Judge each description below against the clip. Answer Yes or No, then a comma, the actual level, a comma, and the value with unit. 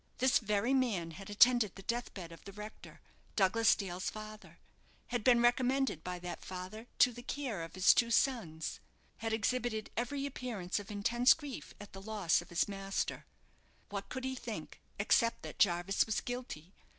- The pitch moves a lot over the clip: No, average, 4.1 semitones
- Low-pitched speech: No, high, 215 Hz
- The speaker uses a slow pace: No, average, 170 wpm